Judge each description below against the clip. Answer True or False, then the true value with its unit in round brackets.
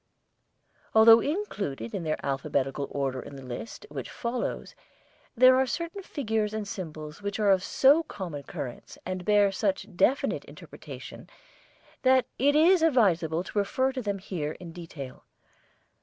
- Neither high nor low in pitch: False (200 Hz)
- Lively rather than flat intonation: True (8.6 semitones)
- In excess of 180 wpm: False (145 wpm)